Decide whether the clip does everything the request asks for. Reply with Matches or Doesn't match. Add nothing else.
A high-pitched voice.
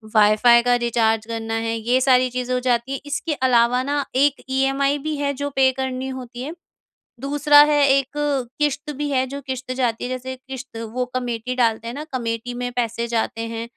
Matches